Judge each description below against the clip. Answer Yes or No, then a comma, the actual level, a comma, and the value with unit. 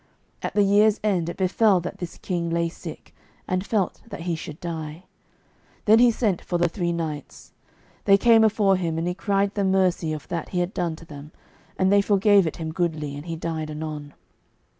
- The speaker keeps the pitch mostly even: No, average, 3.5 semitones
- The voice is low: No, medium, 175 Hz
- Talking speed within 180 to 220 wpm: Yes, fast, 205 wpm